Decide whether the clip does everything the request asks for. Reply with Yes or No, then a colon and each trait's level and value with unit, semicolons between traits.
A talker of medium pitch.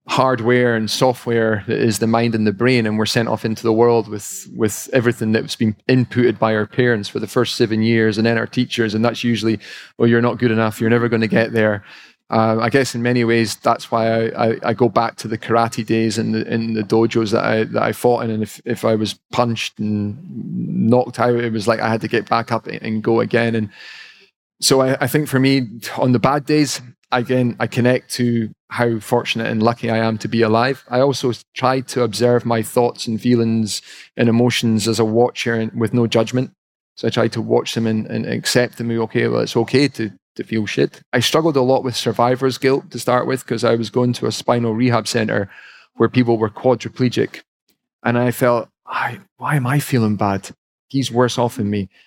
No: low, 115 Hz